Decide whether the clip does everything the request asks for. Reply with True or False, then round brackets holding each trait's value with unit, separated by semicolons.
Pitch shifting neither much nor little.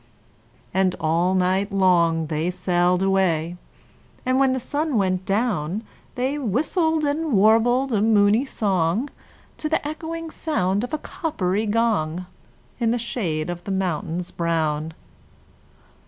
False (6.3 semitones)